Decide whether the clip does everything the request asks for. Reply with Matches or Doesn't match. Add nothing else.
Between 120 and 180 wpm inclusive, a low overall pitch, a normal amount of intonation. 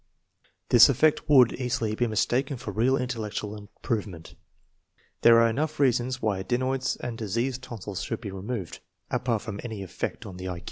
Matches